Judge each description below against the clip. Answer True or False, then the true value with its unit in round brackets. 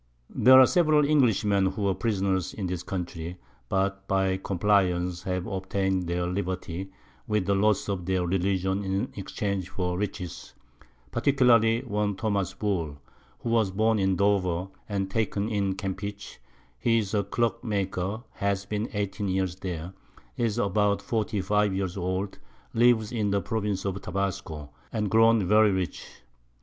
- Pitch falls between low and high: False (100 Hz)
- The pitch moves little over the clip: True (2.2 semitones)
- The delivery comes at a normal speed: True (145 wpm)